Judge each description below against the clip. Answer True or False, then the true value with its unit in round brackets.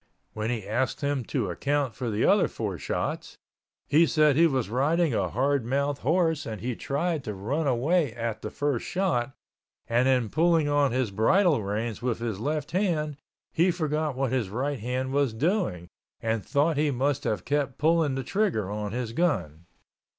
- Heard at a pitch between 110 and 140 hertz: True (135 Hz)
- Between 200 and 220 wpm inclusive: False (180 wpm)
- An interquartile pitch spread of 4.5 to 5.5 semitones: True (4.9 semitones)